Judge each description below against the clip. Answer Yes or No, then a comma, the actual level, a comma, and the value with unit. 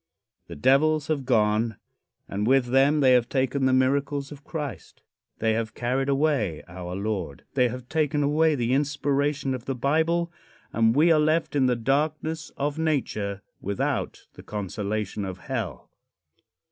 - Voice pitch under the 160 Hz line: Yes, low, 135 Hz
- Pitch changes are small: No, average, 4.8 semitones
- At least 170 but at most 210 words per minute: No, average, 155 wpm